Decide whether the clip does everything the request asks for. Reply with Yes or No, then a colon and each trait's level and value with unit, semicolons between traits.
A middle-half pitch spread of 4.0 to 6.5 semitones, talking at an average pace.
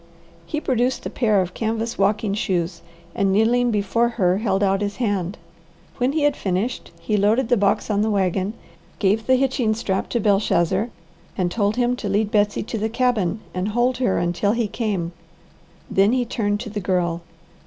No: average, 3.4 semitones; average, 185 wpm